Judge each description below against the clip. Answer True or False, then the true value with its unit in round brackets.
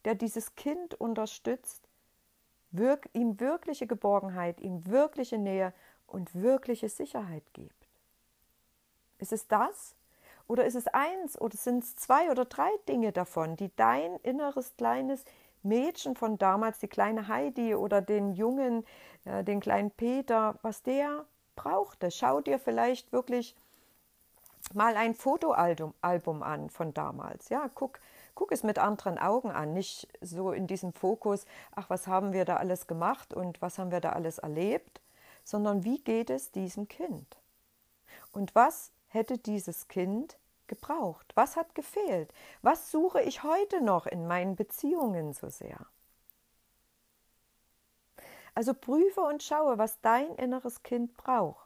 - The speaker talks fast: False (140 wpm)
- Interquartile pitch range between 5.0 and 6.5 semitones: True (5.4 semitones)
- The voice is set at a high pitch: True (225 Hz)